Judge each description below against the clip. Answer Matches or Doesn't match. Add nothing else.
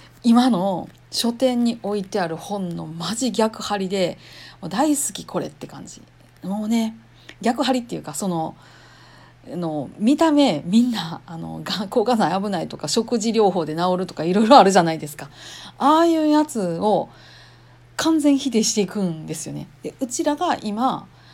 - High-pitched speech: Matches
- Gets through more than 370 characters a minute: Doesn't match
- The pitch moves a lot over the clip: Matches